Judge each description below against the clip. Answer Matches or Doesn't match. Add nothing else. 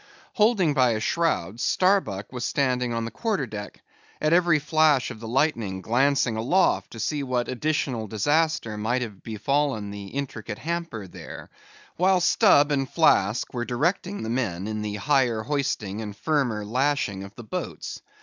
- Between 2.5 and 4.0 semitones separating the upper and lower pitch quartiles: Doesn't match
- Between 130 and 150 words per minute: Doesn't match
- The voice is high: Doesn't match